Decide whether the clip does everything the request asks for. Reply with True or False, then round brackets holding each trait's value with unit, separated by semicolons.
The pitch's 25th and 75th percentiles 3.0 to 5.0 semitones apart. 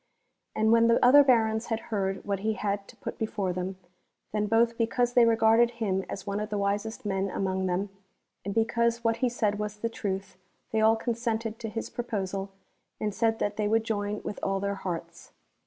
False (2.5 semitones)